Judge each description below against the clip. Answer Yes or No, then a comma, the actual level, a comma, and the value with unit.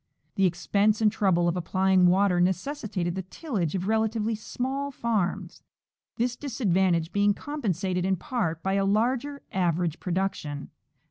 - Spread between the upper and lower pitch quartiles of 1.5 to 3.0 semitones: No, average, 3.9 semitones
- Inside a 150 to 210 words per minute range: No, slow, 135 wpm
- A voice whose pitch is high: Yes, high, 195 Hz